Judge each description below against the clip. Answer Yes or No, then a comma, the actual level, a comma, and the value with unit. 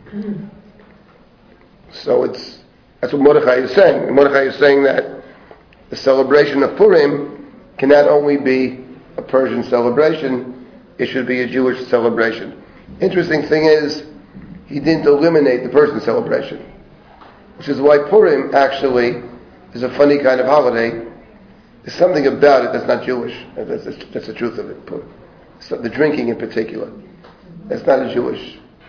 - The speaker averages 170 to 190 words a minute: No, average, 145 wpm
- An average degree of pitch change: Yes, average, 3.5 semitones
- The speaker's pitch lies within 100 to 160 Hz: Yes, medium, 140 Hz